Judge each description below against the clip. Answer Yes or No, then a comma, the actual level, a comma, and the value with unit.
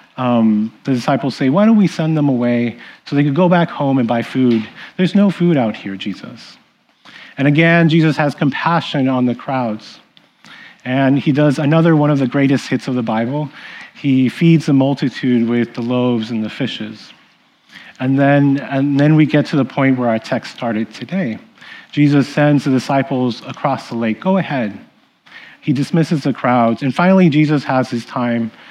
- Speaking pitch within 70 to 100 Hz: No, medium, 140 Hz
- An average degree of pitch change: Yes, average, 3.8 semitones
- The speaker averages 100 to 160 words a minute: No, average, 185 wpm